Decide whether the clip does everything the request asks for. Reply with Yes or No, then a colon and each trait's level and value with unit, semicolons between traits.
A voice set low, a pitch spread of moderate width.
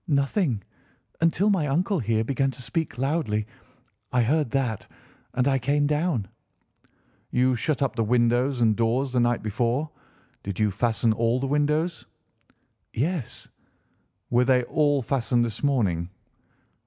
Yes: low, 125 Hz; average, 4.0 semitones